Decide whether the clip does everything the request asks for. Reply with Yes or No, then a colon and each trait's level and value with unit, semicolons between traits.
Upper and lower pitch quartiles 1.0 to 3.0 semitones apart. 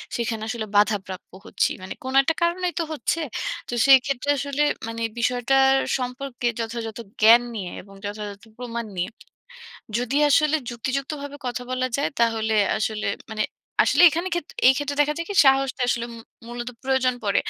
No: average, 3.6 semitones